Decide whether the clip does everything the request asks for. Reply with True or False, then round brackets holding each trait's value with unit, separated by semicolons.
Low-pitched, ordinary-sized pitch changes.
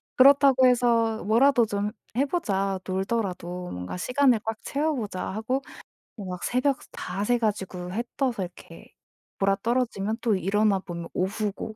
False (215 Hz; 4.4 semitones)